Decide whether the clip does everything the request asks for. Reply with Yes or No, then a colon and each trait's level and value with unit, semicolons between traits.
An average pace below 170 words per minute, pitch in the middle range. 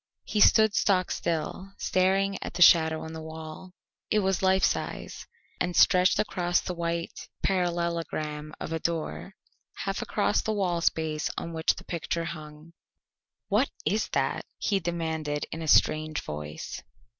Yes: average, 150 wpm; medium, 170 Hz